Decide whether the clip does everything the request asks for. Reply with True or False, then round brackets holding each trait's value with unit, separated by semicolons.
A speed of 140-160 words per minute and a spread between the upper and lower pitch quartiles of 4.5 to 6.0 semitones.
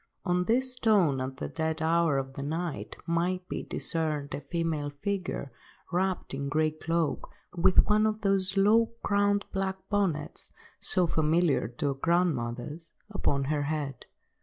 True (150 wpm; 4.8 semitones)